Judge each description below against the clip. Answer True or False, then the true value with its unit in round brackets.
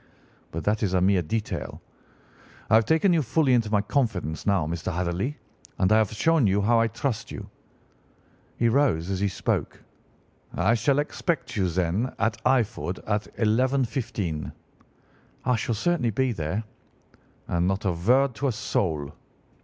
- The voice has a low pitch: True (110 Hz)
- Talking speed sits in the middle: True (160 wpm)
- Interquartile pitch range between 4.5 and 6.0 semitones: True (5.1 semitones)